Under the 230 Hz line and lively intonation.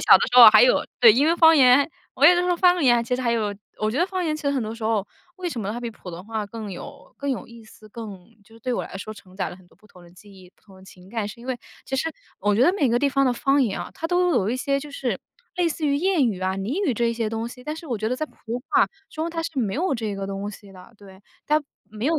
No: high, 240 Hz; wide, 5.7 semitones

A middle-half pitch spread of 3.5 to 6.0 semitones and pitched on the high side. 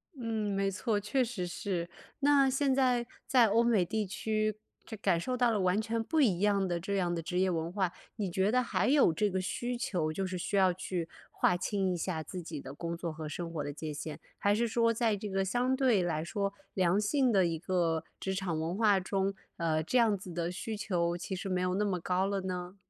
Yes: average, 4.0 semitones; high, 195 Hz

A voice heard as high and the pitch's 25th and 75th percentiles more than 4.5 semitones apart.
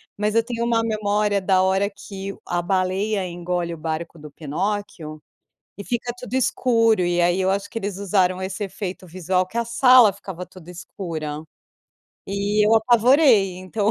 No: high, 195 Hz; average, 3.2 semitones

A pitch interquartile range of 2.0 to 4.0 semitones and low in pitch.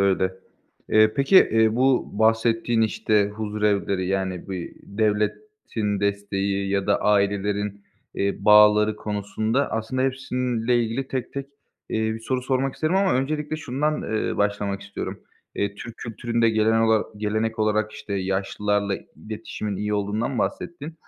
Yes: average, 3.0 semitones; low, 110 Hz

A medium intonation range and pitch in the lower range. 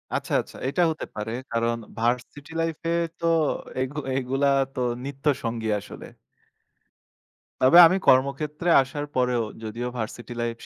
Yes: average, 3.8 semitones; low, 130 Hz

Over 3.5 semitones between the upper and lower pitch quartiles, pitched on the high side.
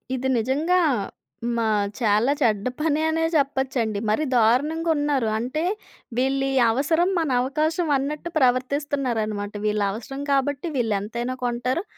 Yes: average, 4.0 semitones; very high, 265 Hz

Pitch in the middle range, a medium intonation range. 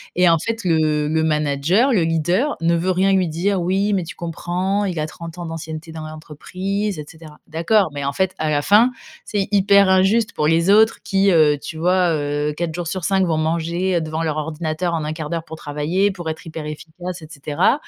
Yes: medium, 170 Hz; average, 3.2 semitones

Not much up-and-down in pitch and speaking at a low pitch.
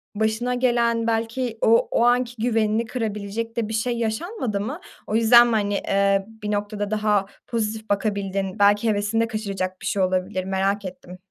No: narrow, 2.3 semitones; high, 215 Hz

